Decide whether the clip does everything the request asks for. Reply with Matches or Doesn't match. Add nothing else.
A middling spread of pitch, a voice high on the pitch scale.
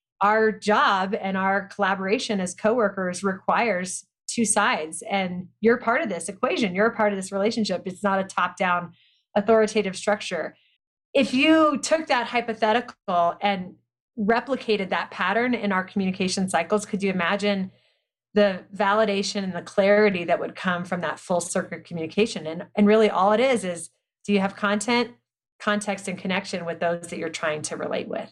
Matches